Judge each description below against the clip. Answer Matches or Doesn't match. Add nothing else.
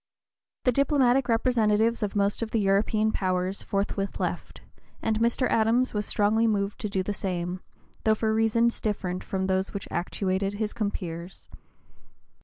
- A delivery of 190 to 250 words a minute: Doesn't match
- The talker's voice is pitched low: Doesn't match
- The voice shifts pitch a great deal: Doesn't match